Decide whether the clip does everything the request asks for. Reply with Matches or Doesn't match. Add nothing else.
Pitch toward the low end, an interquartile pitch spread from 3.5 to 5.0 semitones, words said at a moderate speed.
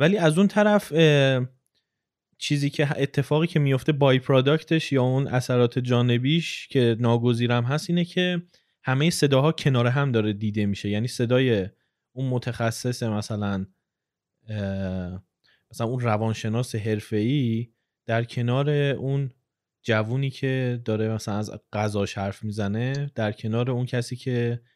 Matches